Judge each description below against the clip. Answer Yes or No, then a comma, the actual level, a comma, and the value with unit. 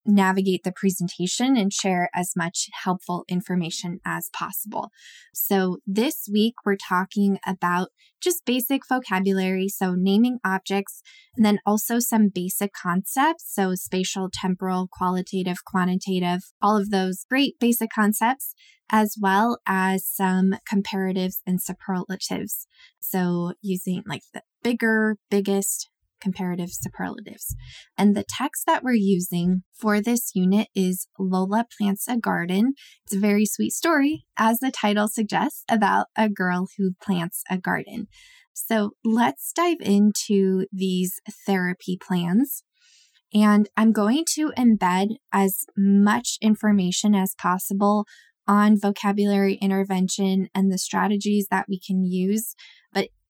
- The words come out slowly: Yes, slow, 125 wpm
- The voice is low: No, high, 200 Hz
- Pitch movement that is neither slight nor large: Yes, average, 3.0 semitones